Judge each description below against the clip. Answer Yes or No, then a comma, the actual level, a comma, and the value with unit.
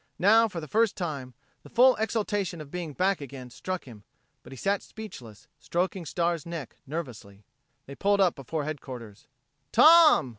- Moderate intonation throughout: No, wide, 7.0 semitones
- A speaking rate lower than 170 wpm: Yes, average, 160 wpm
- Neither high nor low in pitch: Yes, medium, 170 Hz